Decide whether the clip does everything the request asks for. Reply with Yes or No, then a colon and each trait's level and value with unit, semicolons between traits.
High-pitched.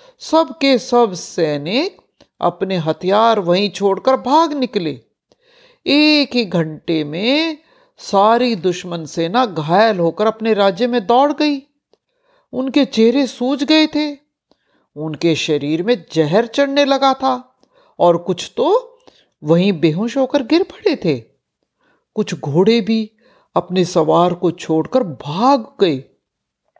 Yes: high, 230 Hz